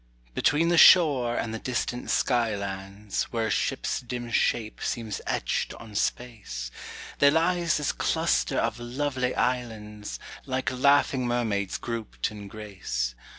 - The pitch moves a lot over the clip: No, average, 3.6 semitones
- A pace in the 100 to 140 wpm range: Yes, slow, 135 wpm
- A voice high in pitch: No, low, 120 Hz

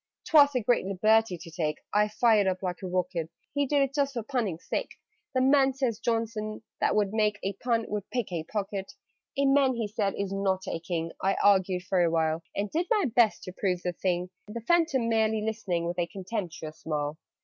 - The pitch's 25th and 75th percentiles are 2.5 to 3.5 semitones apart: No, average, 4.6 semitones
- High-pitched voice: Yes, high, 205 Hz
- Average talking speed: No, fast, 210 wpm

